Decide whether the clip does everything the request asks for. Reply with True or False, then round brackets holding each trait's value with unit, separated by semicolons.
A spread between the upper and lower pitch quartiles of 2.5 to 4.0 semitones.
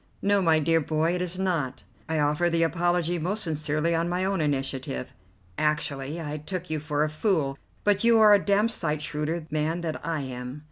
True (2.9 semitones)